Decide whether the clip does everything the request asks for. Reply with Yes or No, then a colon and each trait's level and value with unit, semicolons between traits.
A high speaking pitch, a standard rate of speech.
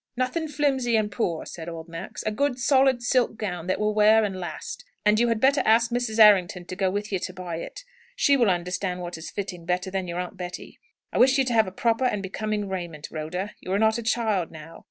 No: high, 210 Hz; fast, 235 wpm